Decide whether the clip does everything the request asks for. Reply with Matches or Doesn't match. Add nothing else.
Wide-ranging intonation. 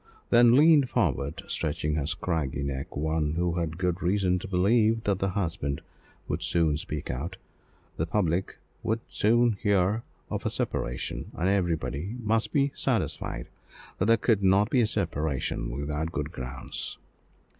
Matches